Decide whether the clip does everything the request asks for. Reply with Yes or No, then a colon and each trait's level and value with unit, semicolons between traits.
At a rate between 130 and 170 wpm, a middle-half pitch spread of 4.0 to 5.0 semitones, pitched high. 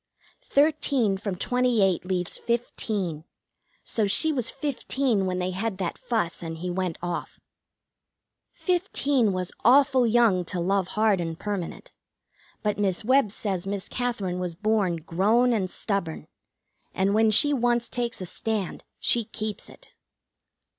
Yes: average, 140 wpm; average, 4.6 semitones; high, 210 Hz